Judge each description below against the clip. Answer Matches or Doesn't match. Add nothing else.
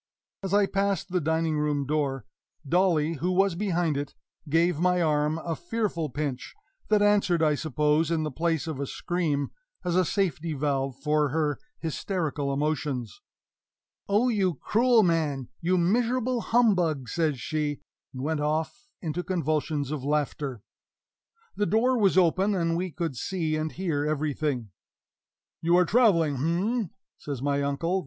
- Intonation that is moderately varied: Matches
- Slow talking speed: Doesn't match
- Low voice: Doesn't match